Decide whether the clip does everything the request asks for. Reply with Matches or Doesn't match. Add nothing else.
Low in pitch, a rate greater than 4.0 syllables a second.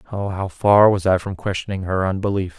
Matches